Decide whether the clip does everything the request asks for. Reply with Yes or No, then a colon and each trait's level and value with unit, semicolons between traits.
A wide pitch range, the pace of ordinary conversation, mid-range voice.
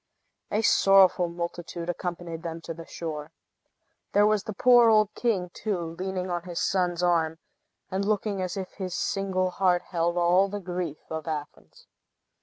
No: narrow, 2.5 semitones; average, 160 wpm; medium, 180 Hz